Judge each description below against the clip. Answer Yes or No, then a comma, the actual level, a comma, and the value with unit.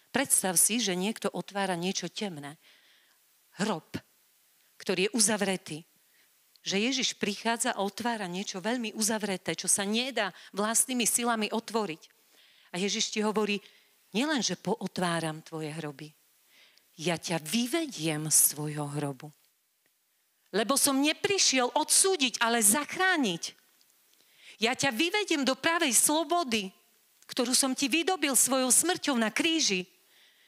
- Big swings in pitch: Yes, wide, 6.3 semitones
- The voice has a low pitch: No, high, 220 Hz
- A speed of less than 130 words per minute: Yes, average, 115 wpm